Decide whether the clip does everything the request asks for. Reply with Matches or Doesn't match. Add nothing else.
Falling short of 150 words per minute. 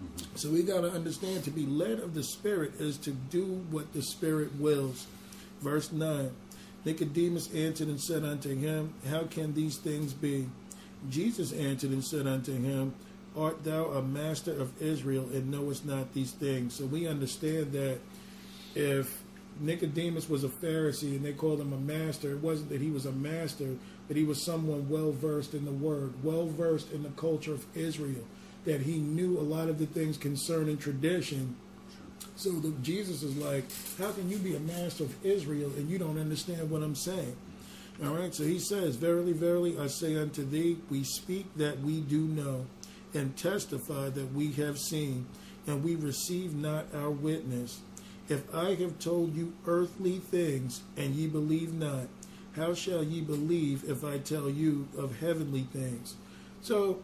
Doesn't match